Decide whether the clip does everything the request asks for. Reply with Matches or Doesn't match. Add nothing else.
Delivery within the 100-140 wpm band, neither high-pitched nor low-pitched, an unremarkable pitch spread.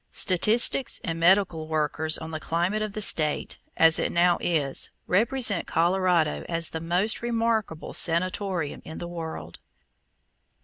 Matches